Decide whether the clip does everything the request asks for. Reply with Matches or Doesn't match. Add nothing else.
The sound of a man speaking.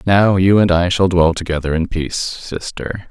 Matches